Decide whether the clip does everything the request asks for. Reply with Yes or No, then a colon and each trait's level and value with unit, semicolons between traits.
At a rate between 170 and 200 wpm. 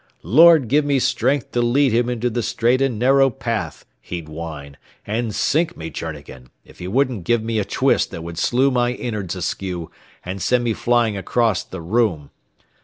Yes: average, 180 wpm